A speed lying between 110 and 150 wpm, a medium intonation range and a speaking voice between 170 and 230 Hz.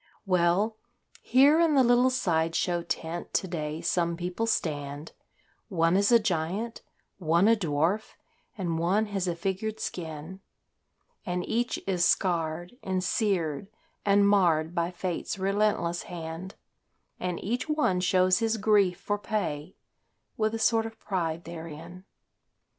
Yes: slow, 135 wpm; average, 4.1 semitones; medium, 185 Hz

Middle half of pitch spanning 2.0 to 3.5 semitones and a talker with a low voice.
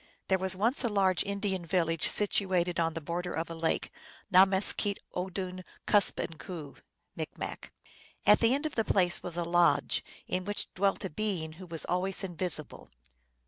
No: average, 2.7 semitones; medium, 185 Hz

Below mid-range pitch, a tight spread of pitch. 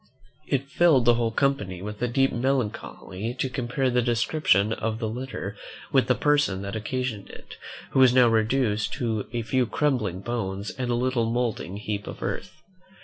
No: low, 120 Hz; average, 3.5 semitones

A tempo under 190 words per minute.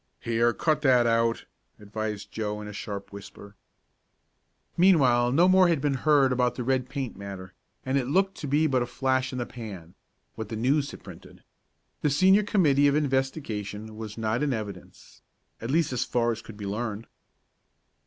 Yes: average, 180 wpm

